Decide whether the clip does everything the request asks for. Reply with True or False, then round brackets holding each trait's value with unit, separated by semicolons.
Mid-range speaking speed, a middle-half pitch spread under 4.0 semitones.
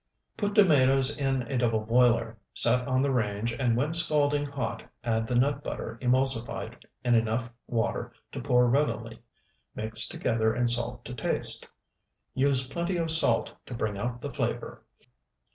True (150 wpm; 3.3 semitones)